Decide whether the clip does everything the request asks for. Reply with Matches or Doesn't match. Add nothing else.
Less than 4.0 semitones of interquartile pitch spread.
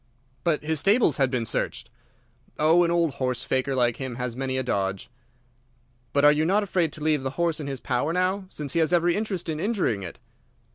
Doesn't match